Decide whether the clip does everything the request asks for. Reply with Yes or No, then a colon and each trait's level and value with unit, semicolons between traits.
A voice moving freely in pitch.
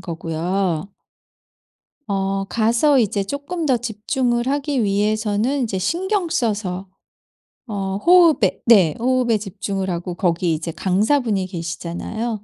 No: average, 4.6 semitones